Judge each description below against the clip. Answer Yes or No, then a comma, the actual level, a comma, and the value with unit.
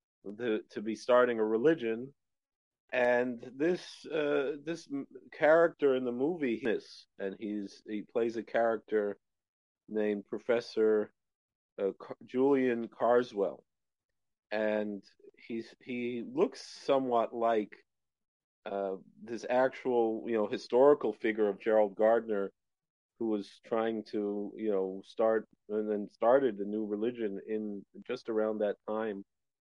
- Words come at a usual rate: No, slow, 120 wpm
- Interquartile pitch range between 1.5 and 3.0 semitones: Yes, average, 2.7 semitones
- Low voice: Yes, low, 110 Hz